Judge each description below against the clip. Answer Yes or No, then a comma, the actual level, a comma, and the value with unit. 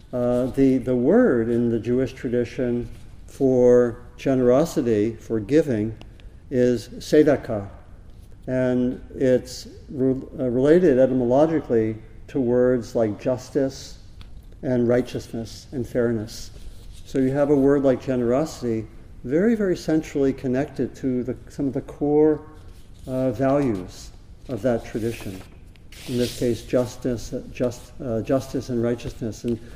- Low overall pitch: Yes, low, 125 Hz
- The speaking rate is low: Yes, slow, 120 wpm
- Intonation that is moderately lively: Yes, average, 3.0 semitones